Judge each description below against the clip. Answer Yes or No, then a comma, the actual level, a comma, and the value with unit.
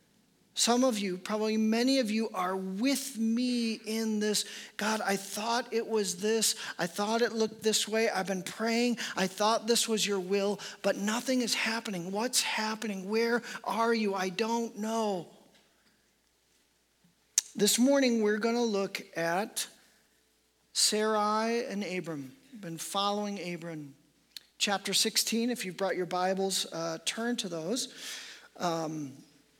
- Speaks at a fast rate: No, average, 140 wpm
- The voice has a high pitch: Yes, high, 215 Hz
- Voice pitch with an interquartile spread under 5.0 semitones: Yes, average, 3.2 semitones